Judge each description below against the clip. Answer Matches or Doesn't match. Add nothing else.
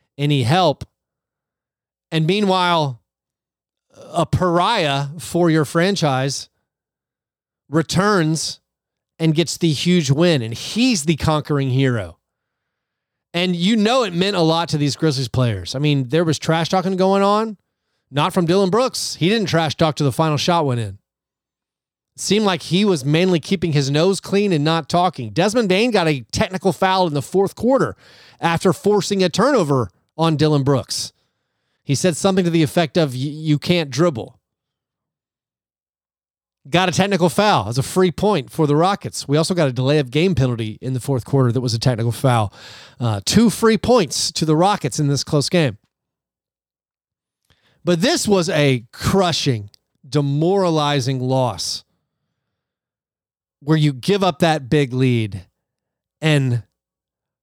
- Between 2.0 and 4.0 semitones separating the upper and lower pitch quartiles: Doesn't match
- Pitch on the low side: Doesn't match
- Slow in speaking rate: Doesn't match